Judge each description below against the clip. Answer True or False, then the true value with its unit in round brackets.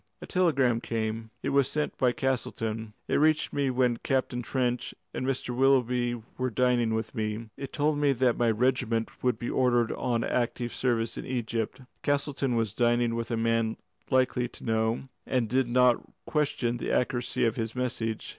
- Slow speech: False (175 wpm)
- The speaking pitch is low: True (120 Hz)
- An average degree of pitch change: False (2.2 semitones)